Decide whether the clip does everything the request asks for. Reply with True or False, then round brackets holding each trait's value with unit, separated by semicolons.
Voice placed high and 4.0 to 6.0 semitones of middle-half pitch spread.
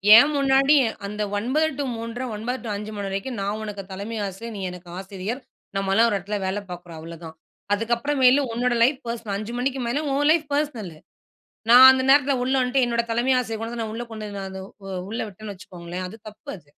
True (225 Hz; 4.3 semitones)